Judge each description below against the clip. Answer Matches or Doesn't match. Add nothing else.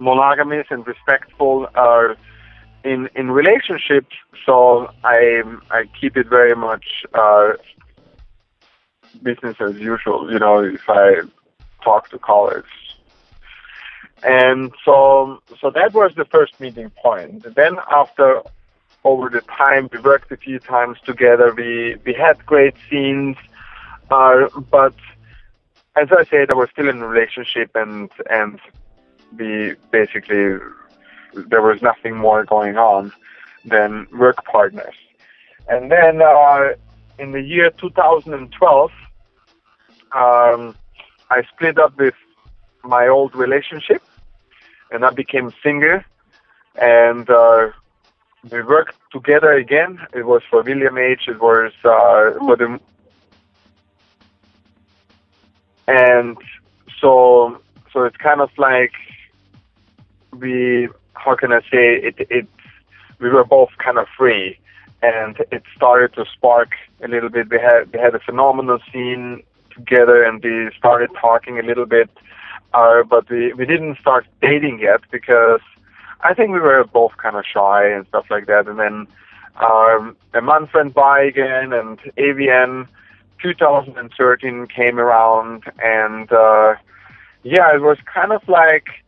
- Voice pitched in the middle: Doesn't match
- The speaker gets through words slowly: Matches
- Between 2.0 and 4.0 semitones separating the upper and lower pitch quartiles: Matches